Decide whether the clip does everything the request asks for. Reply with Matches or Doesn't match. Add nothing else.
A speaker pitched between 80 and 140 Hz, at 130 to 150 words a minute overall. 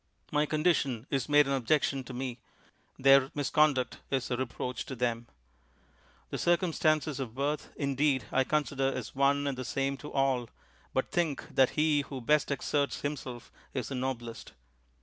Doesn't match